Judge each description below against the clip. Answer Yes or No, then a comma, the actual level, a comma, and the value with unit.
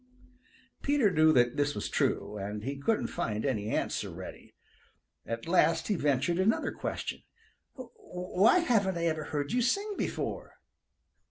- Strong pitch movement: Yes, wide, 7.9 semitones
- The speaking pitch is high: No, medium, 165 Hz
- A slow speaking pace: No, average, 145 wpm